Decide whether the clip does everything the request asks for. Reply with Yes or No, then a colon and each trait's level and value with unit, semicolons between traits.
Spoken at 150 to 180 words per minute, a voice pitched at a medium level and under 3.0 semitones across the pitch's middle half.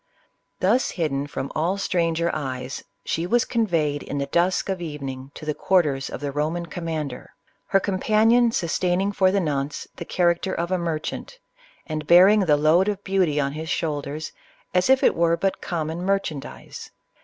No: average, 170 wpm; medium, 170 Hz; average, 4.0 semitones